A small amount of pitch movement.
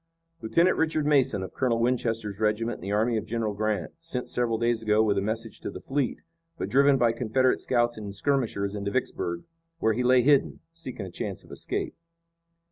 No: average, 3.4 semitones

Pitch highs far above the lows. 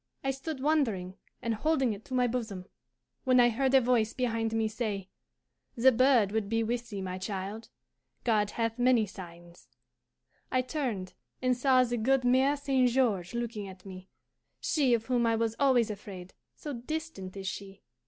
No: average, 4.1 semitones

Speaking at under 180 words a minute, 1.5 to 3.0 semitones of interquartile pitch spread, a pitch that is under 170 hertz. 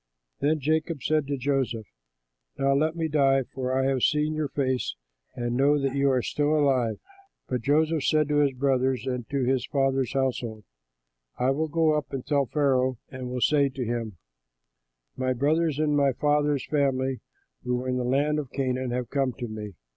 No: average, 185 wpm; narrow, 2.5 semitones; low, 135 Hz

